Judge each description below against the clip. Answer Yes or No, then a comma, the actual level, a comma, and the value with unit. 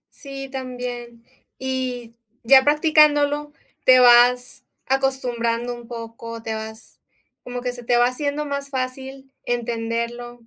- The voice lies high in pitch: Yes, very high, 250 Hz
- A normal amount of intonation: No, narrow, 2.1 semitones